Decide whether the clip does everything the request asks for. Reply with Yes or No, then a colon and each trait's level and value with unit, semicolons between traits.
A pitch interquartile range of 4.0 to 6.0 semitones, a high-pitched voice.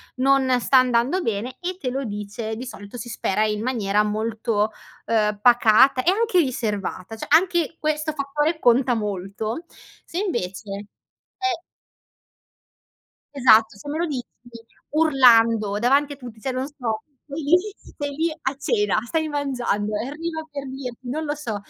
Yes: average, 5.3 semitones; very high, 255 Hz